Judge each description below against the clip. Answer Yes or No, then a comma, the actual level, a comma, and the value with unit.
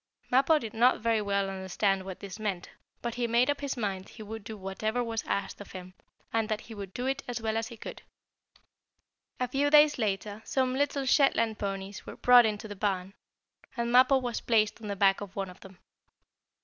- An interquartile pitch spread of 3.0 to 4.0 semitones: Yes, average, 3.7 semitones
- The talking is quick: Yes, fast, 210 wpm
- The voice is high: Yes, high, 220 Hz